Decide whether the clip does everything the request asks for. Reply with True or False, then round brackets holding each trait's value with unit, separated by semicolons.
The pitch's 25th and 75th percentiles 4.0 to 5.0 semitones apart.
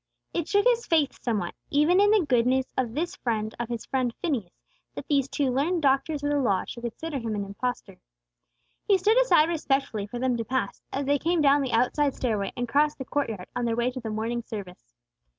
True (4.4 semitones)